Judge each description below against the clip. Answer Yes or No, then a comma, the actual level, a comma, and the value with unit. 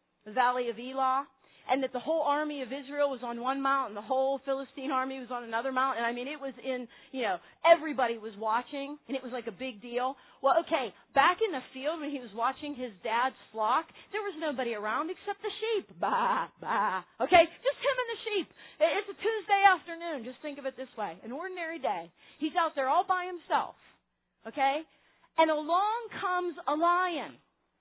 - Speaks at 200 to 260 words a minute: Yes, fast, 205 wpm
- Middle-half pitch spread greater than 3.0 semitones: Yes, average, 5.1 semitones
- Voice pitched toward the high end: Yes, very high, 280 Hz